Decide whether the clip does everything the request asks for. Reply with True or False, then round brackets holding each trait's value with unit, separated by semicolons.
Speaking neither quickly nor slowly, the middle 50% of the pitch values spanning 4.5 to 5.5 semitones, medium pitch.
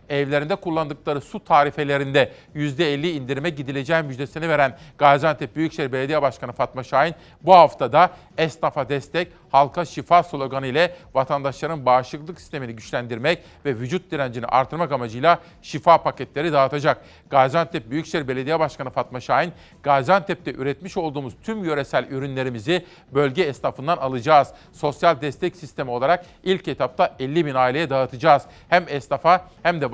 False (130 wpm; 3.7 semitones; 150 Hz)